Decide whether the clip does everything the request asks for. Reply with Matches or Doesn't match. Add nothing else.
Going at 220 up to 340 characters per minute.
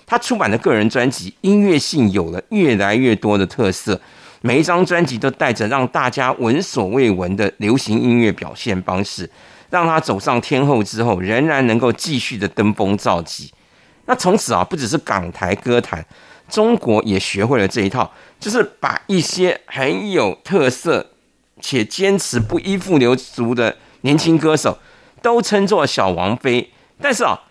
Matches